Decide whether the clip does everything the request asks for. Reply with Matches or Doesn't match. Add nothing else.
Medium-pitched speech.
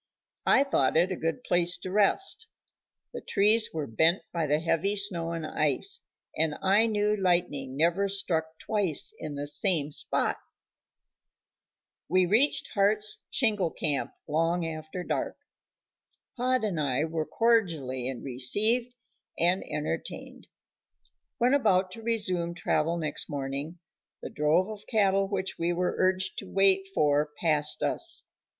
Matches